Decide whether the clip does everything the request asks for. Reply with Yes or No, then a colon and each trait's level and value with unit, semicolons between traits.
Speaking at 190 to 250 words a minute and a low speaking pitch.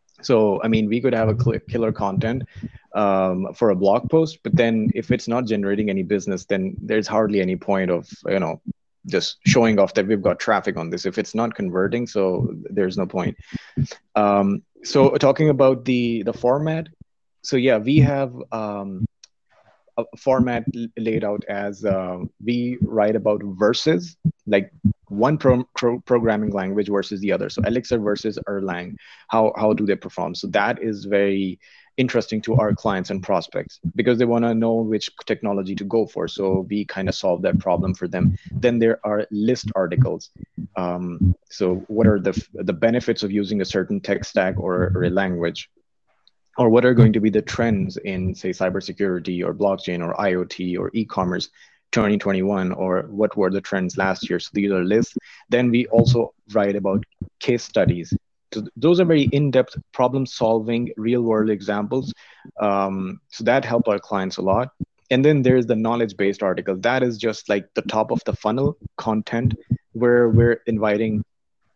No: average, 175 wpm; low, 110 Hz